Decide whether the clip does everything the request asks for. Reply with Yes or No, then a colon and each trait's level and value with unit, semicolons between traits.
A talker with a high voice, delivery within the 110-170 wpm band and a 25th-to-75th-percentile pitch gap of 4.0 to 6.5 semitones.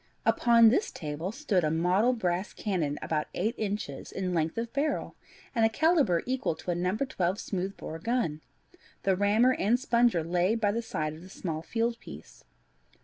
No: high, 195 Hz; average, 180 wpm; average, 5.3 semitones